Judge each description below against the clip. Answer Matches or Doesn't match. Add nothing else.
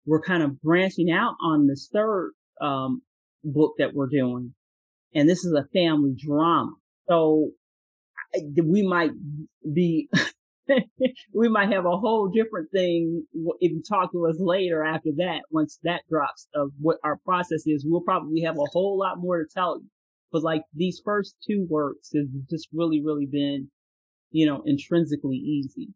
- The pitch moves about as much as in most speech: Matches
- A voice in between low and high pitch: Matches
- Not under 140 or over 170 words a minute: Matches